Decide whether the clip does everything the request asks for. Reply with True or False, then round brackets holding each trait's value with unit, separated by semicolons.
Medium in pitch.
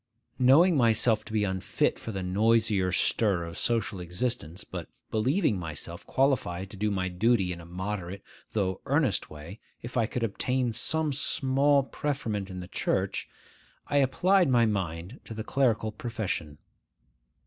False (110 Hz)